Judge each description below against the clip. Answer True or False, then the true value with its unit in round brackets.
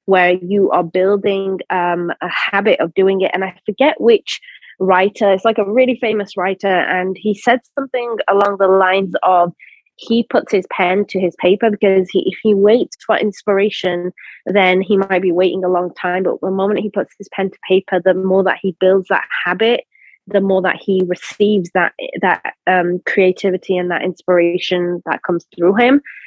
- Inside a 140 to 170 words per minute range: False (190 wpm)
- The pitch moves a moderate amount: False (2.1 semitones)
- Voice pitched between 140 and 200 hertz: True (190 Hz)